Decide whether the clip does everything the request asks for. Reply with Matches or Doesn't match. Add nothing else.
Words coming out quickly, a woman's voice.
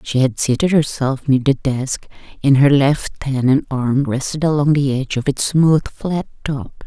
Doesn't match